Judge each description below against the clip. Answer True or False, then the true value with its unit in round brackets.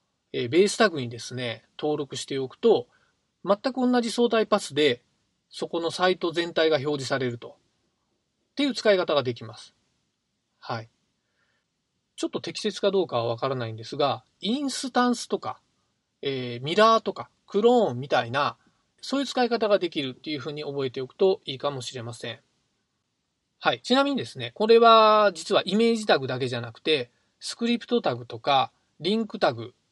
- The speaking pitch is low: False (165 Hz)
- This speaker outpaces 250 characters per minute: True (340 characters per minute)